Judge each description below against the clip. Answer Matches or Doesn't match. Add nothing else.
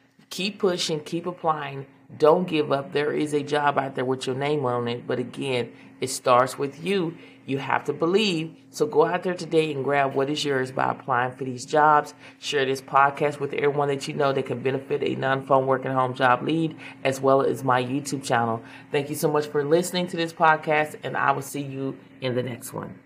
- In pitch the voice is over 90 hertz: Matches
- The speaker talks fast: Matches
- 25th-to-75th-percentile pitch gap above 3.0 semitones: Doesn't match